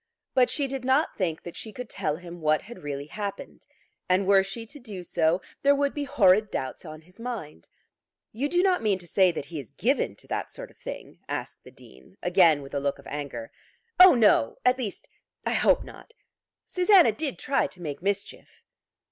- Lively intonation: Yes, wide, 8.3 semitones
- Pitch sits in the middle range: No, high, 195 Hz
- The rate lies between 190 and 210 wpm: Yes, fast, 205 wpm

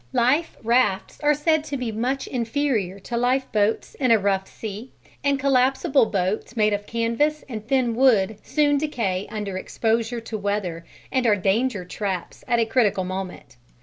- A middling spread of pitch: Yes, average, 4.4 semitones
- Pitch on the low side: No, high, 230 Hz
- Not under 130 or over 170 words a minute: Yes, average, 160 wpm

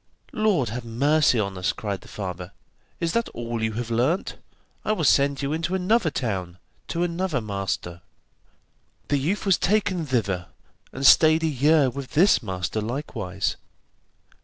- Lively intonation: Yes, wide, 7.7 semitones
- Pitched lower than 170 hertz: Yes, low, 135 Hz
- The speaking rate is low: No, average, 155 wpm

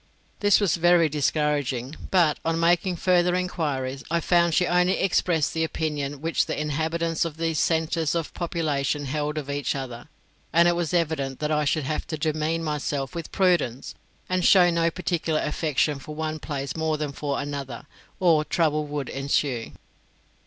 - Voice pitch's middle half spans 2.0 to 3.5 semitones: Yes, average, 2.7 semitones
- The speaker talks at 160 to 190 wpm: Yes, average, 165 wpm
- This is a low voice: No, medium, 155 Hz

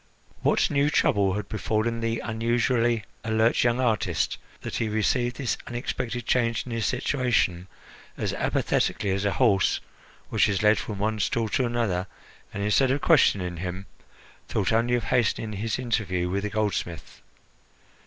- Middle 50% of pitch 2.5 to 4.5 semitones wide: Yes, average, 3.1 semitones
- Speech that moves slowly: No, average, 155 wpm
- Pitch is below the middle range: Yes, low, 110 Hz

